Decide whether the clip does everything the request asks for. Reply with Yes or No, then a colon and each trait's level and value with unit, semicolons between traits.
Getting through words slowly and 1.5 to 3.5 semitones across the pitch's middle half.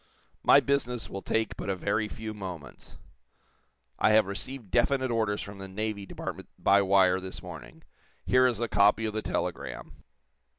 No: average, 165 wpm; average, 2.8 semitones